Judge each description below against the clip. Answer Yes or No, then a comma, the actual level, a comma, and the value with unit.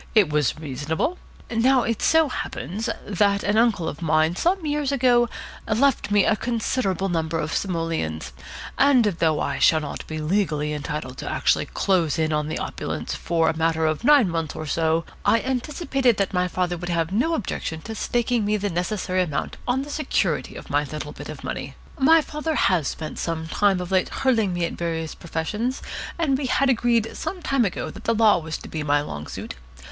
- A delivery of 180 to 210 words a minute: Yes, average, 200 wpm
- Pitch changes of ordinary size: No, wide, 7.0 semitones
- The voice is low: No, high, 190 Hz